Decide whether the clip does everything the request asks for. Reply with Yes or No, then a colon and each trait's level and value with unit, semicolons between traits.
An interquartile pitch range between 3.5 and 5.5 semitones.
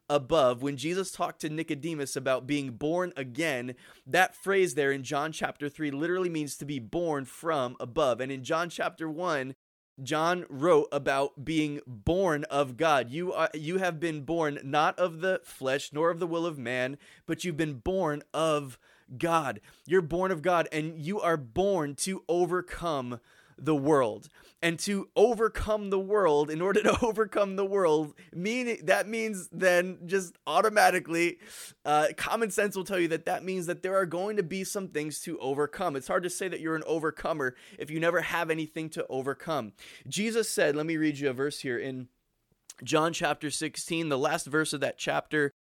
Yes: average, 3.8 semitones